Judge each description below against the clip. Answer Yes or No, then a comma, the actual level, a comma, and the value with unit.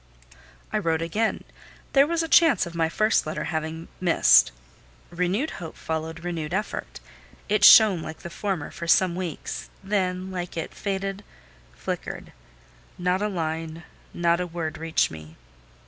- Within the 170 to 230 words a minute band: No, average, 150 wpm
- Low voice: No, medium, 175 Hz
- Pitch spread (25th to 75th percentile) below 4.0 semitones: Yes, average, 3.2 semitones